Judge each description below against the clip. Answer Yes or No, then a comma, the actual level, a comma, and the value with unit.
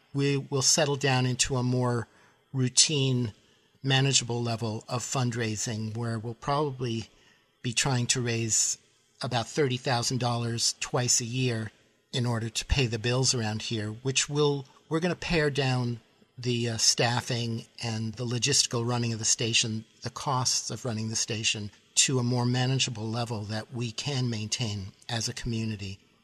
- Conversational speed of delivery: Yes, average, 155 wpm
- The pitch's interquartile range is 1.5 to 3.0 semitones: Yes, narrow, 2.5 semitones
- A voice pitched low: Yes, low, 120 Hz